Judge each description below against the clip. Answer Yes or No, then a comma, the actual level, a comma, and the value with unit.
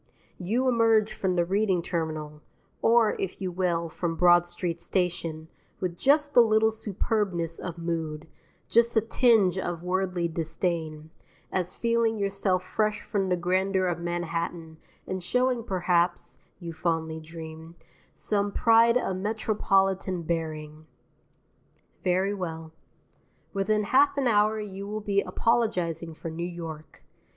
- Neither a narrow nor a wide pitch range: Yes, average, 4.0 semitones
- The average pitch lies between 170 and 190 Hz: Yes, medium, 185 Hz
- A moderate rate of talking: No, slow, 130 wpm